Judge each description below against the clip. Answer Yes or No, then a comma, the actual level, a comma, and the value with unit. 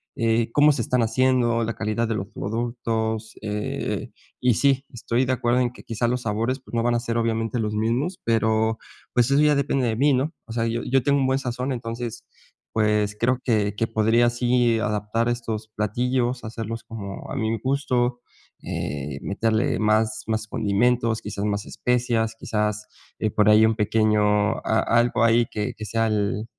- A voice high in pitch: No, low, 115 Hz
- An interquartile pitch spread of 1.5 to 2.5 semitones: Yes, narrow, 2.1 semitones